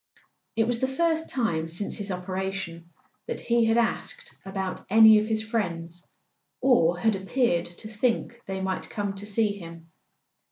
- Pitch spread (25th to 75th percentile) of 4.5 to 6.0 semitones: No, average, 4.1 semitones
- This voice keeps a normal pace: Yes, average, 160 wpm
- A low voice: No, high, 205 Hz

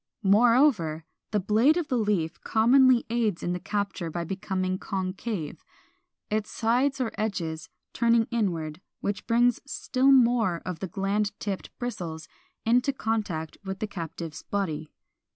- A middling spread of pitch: Yes, average, 5.0 semitones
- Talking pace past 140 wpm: No, slow, 135 wpm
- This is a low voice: No, high, 205 Hz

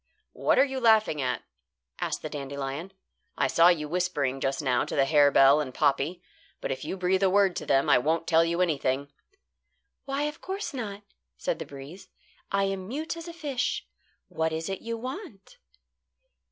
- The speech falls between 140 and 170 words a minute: No, average, 180 wpm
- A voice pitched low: No, medium, 175 Hz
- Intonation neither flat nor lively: No, wide, 7.9 semitones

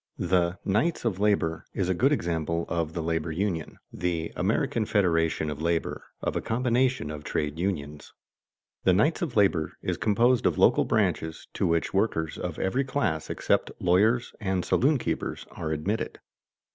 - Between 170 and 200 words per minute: No, average, 160 wpm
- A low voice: Yes, very low, 90 Hz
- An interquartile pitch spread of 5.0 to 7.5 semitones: Yes, wide, 5.4 semitones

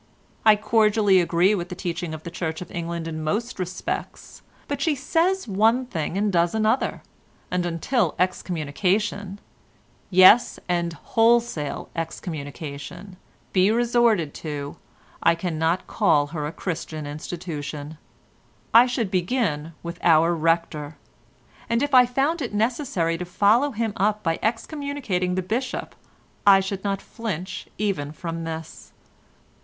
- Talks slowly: Yes, slow, 130 wpm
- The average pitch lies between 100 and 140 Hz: No, medium, 185 Hz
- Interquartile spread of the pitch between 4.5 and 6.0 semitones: Yes, average, 5.1 semitones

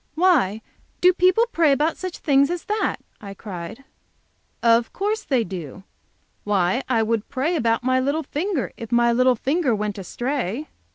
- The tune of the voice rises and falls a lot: Yes, wide, 6.5 semitones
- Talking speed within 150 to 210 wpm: Yes, average, 160 wpm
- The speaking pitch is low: No, very high, 255 Hz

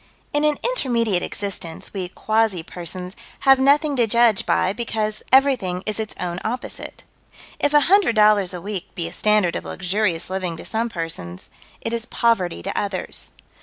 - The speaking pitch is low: No, high, 210 Hz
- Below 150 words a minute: No, average, 165 wpm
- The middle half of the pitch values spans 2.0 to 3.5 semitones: No, average, 4.6 semitones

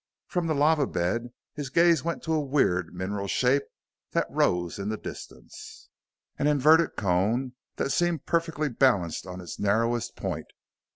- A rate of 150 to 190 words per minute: Yes, average, 155 wpm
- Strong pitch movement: Yes, wide, 7.6 semitones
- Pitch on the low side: Yes, low, 130 Hz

